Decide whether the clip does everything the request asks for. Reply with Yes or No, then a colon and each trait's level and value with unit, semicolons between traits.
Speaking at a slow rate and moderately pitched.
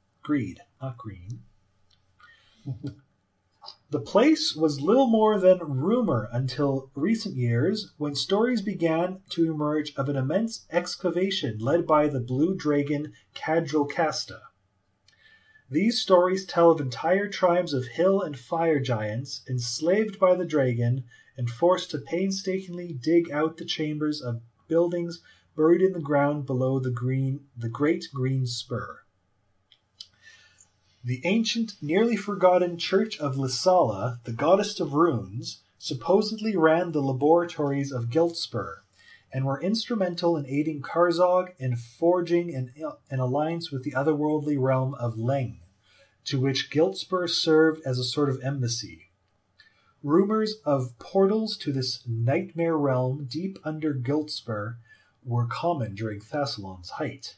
Yes: slow, 130 wpm; medium, 150 Hz